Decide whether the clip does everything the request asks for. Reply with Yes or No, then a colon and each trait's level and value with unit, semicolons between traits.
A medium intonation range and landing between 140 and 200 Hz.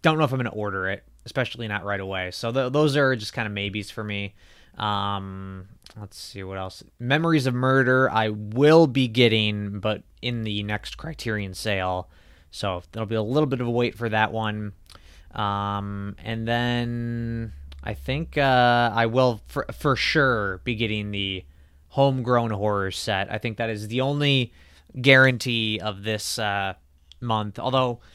No: average, 3.5 semitones; low, 110 Hz